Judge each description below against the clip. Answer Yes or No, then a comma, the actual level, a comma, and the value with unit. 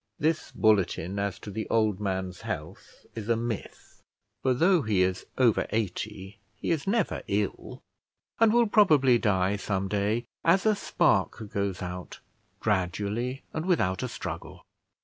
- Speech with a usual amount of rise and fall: No, wide, 5.8 semitones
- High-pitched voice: No, low, 110 Hz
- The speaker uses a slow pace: No, average, 150 wpm